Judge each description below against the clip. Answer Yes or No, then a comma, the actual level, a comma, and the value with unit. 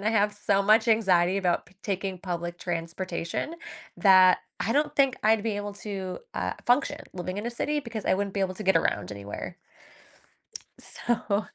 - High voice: Yes, high, 200 Hz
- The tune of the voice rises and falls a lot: No, average, 3.4 semitones